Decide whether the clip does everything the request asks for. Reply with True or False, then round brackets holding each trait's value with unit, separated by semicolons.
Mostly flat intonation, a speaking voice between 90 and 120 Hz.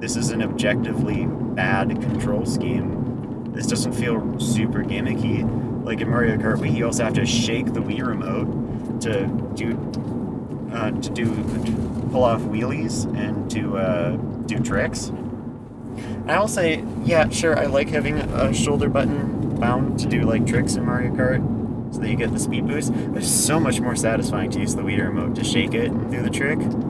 True (1.1 semitones; 115 Hz)